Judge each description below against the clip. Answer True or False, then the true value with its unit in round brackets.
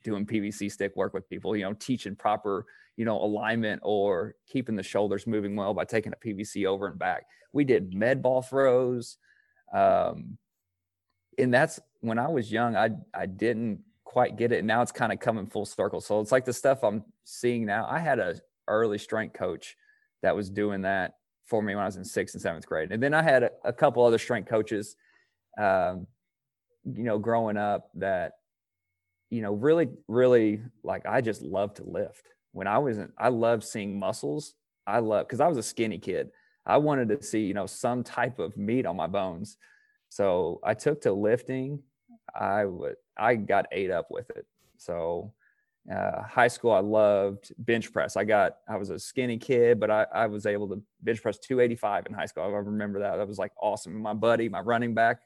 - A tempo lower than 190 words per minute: False (200 wpm)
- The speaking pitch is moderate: False (115 Hz)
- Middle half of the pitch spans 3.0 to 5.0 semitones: True (4.0 semitones)